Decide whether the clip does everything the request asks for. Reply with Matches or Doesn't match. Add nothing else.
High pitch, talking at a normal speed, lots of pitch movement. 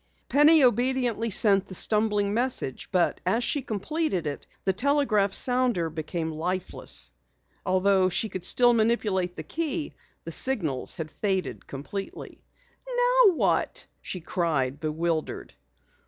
Doesn't match